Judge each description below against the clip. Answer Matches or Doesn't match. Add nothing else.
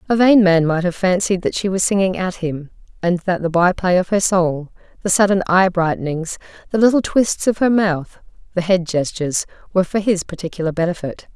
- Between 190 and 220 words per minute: Matches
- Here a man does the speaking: Doesn't match